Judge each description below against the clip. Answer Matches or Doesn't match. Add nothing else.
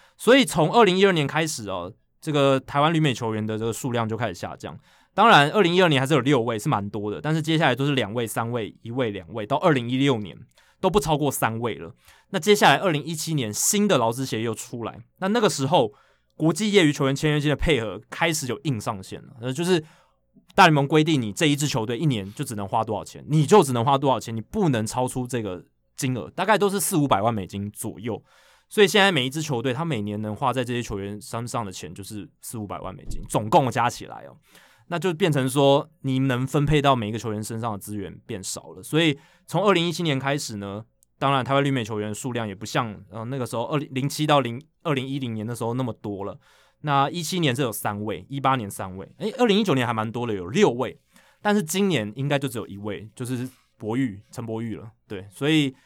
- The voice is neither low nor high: Doesn't match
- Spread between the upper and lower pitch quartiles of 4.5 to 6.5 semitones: Matches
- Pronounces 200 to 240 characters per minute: Doesn't match